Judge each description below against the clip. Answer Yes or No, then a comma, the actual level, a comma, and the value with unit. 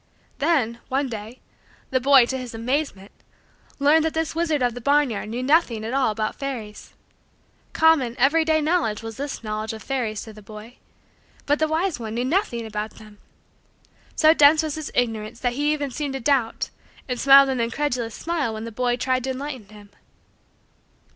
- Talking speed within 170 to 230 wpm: Yes, average, 180 wpm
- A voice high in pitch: Yes, very high, 255 Hz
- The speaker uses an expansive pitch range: No, average, 4.6 semitones